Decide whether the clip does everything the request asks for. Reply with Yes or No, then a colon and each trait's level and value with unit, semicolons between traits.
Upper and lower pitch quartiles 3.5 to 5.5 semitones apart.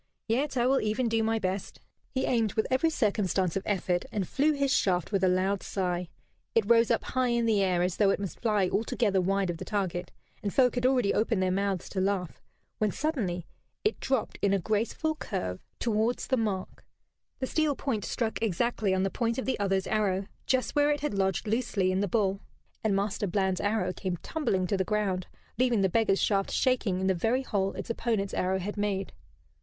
Yes: average, 3.8 semitones